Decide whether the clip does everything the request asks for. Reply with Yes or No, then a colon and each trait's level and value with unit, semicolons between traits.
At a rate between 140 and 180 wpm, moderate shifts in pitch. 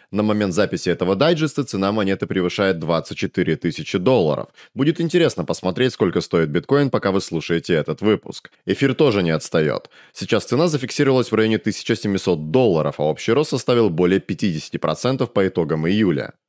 No: average, 155 wpm; wide, 6.4 semitones